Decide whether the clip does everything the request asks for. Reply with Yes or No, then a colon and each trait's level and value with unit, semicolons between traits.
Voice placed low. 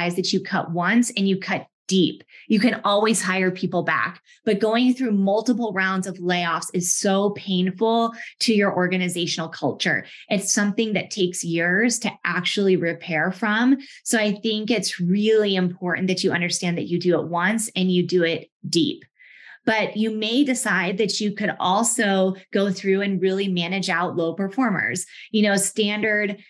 No: high, 195 Hz